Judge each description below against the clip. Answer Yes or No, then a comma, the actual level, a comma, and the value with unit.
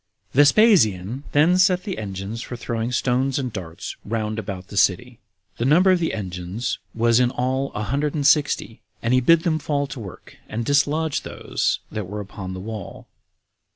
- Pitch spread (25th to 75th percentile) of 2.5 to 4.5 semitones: No, wide, 5.5 semitones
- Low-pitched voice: Yes, low, 120 Hz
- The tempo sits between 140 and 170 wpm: No, average, 180 wpm